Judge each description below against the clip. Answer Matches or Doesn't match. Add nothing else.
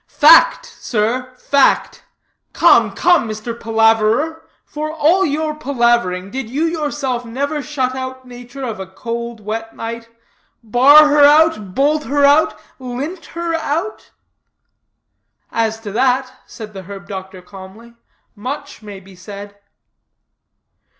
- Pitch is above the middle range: Matches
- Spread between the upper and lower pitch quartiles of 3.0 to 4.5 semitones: Doesn't match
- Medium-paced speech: Doesn't match